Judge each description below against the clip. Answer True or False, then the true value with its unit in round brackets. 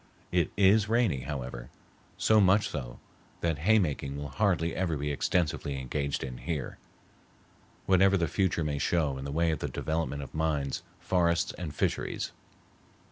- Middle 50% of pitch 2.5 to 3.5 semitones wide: False (4.4 semitones)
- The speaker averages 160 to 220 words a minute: False (150 wpm)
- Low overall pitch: True (80 Hz)